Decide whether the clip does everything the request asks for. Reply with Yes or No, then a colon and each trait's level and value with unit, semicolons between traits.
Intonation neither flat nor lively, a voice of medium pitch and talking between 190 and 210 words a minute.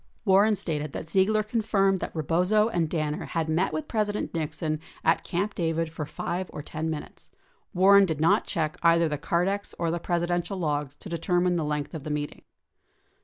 Yes: average, 3.7 semitones; medium, 170 Hz; average, 195 wpm